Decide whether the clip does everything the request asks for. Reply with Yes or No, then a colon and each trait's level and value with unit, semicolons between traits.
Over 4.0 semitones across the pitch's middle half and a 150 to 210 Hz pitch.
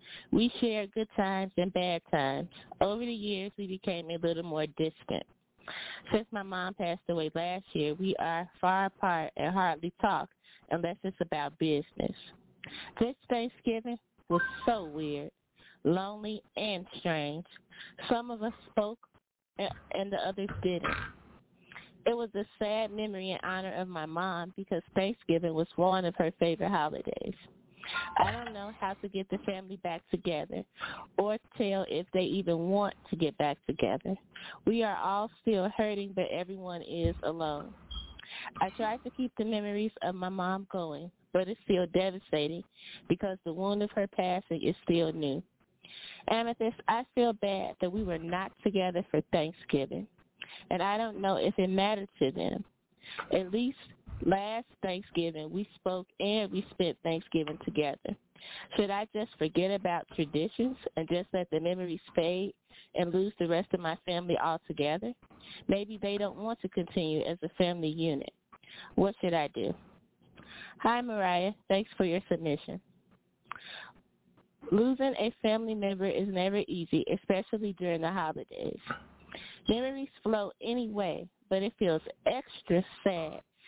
No: average, 3.6 semitones; high, 190 Hz